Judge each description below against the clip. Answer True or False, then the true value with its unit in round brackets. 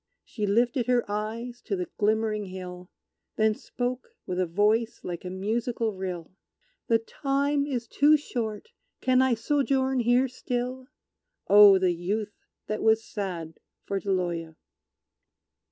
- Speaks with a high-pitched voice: True (220 Hz)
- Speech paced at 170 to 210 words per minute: False (135 wpm)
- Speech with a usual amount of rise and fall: True (4.5 semitones)